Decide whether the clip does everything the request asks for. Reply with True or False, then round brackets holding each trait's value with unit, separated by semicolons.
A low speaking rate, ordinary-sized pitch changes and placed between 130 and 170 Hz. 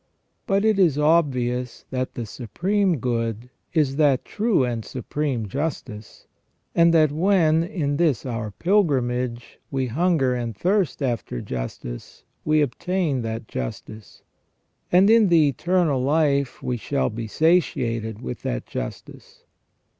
False (130 wpm; 6.0 semitones; 140 Hz)